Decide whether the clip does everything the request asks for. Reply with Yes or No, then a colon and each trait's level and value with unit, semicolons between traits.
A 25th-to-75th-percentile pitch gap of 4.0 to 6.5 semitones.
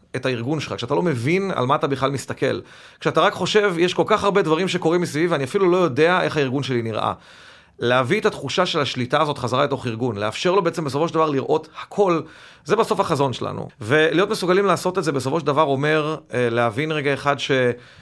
Yes: average, 4.9 semitones